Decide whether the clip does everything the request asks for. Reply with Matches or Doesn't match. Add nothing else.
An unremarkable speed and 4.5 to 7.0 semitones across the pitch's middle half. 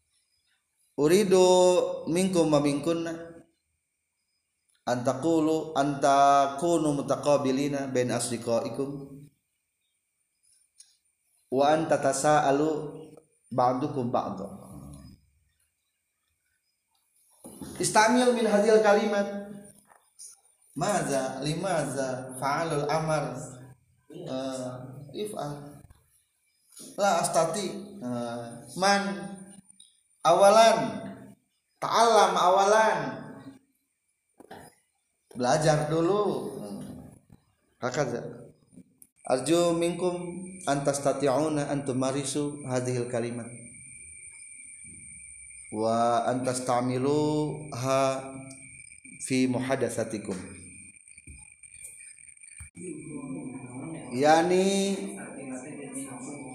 Doesn't match